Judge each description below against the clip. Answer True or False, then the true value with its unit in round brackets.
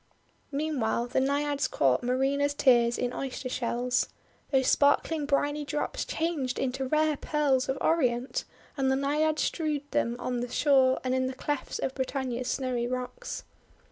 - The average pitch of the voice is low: False (265 Hz)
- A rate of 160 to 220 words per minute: False (150 wpm)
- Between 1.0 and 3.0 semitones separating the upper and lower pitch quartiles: True (2.5 semitones)